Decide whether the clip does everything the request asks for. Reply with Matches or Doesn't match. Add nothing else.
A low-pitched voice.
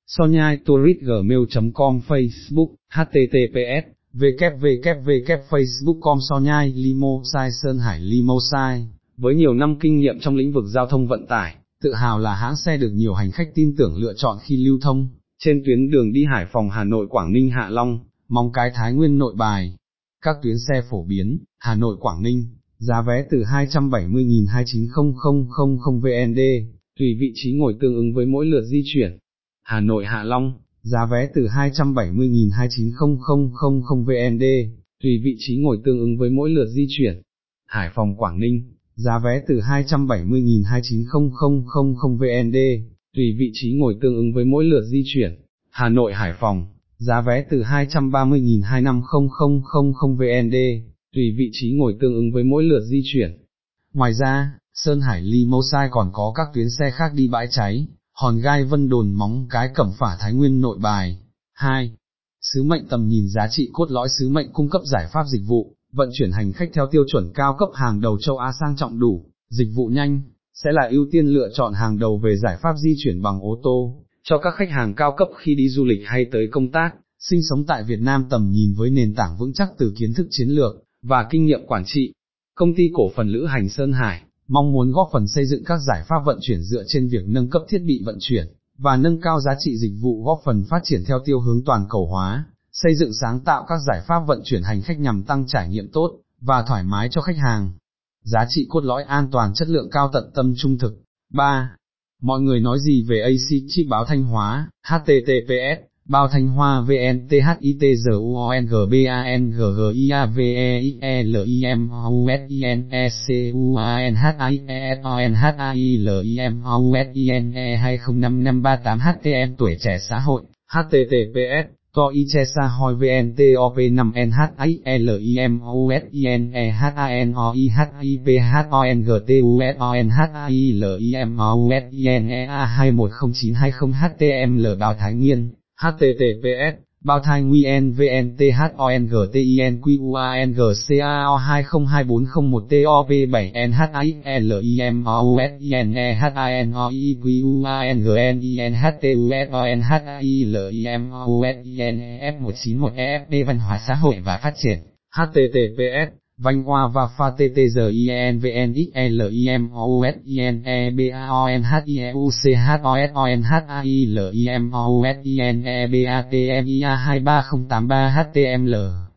Matches